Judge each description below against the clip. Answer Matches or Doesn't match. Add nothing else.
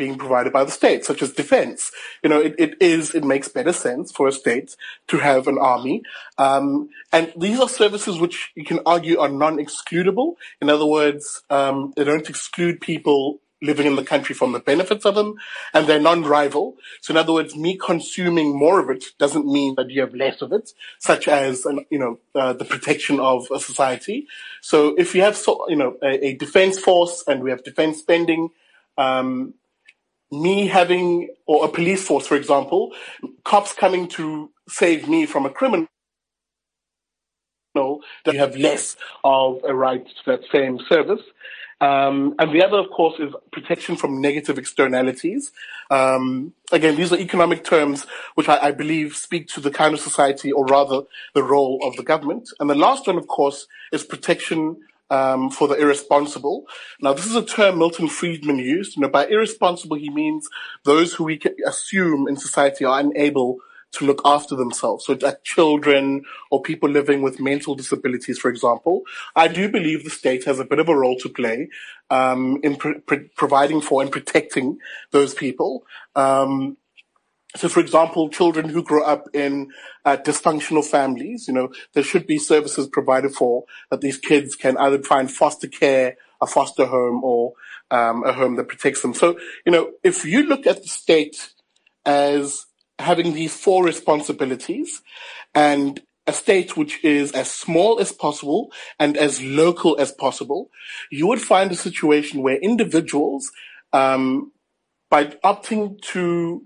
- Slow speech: Doesn't match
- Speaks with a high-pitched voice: Doesn't match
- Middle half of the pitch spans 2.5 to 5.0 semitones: Matches